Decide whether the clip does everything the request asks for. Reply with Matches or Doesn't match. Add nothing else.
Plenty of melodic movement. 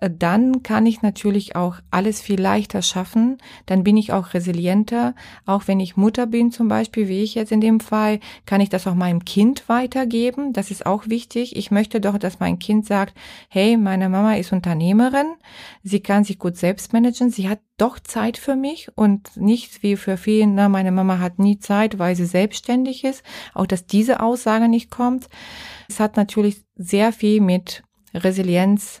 Doesn't match